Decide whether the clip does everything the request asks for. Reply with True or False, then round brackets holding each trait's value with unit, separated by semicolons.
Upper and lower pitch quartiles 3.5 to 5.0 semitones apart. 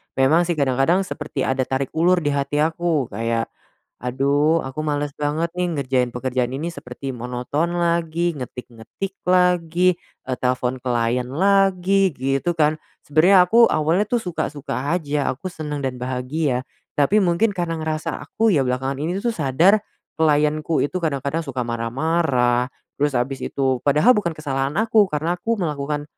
True (4.6 semitones)